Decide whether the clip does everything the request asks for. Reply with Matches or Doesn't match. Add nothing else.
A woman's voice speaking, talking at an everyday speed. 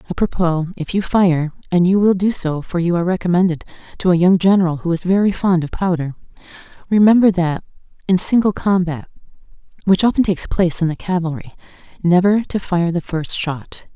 Matches